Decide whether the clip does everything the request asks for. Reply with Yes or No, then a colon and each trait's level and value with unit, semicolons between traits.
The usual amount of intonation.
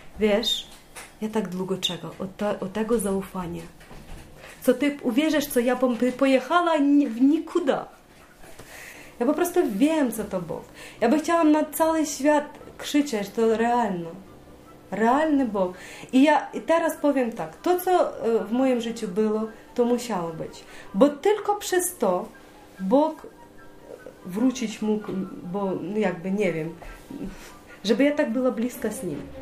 No: wide, 6.6 semitones